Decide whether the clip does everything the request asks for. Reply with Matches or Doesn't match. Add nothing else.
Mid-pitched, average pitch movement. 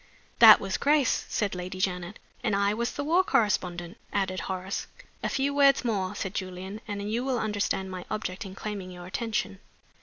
Doesn't match